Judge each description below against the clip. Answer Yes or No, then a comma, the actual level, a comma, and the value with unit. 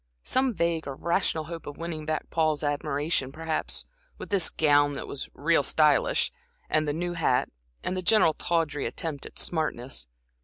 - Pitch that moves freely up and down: No, narrow, 2.6 semitones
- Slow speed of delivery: No, average, 160 wpm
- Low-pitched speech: No, medium, 155 Hz